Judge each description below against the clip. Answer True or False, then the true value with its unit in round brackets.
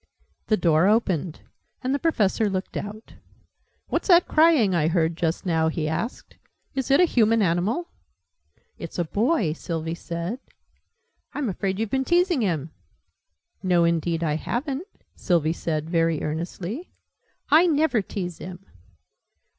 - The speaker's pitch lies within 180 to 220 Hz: True (190 Hz)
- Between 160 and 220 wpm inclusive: False (140 wpm)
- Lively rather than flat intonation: True (7.3 semitones)